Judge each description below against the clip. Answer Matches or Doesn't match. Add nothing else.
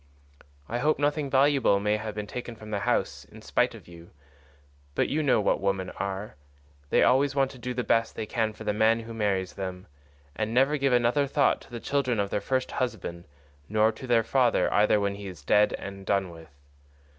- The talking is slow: Doesn't match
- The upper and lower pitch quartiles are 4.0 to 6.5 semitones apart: Matches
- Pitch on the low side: Matches